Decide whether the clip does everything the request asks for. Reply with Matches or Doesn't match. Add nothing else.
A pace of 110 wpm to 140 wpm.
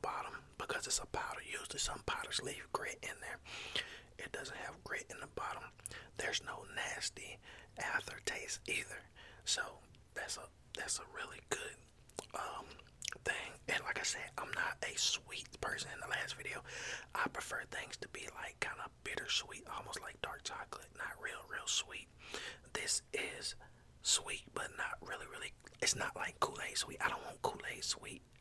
Doesn't match